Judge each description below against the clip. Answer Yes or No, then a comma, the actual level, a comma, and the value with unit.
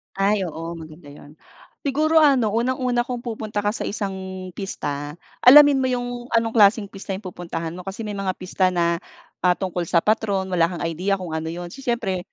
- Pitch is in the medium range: No, high, 195 Hz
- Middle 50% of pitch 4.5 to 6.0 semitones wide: Yes, wide, 5.4 semitones